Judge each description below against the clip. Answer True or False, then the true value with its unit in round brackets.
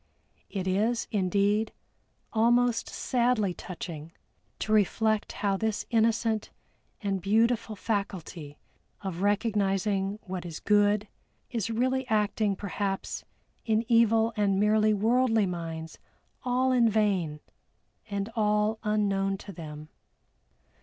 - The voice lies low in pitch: False (210 Hz)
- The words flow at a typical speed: False (105 wpm)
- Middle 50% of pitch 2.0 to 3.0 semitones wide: True (2.5 semitones)